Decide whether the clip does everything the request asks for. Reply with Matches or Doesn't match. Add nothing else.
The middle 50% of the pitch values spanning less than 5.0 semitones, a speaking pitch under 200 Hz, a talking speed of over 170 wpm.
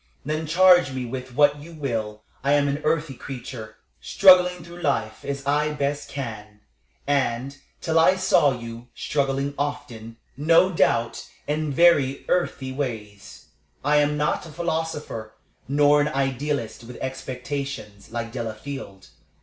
Doesn't match